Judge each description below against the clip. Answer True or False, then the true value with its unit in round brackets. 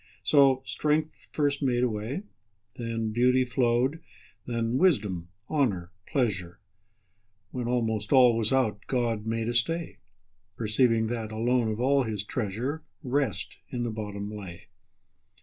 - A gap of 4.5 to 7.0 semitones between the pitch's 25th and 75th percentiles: False (3.5 semitones)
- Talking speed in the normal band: False (115 wpm)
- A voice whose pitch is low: True (115 Hz)